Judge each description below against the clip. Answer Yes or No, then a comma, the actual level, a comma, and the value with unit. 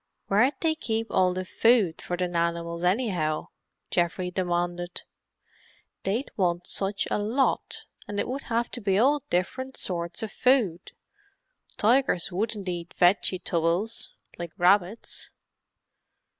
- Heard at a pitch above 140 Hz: Yes, medium, 185 Hz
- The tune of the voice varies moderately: Yes, average, 4.4 semitones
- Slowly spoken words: Yes, slow, 130 wpm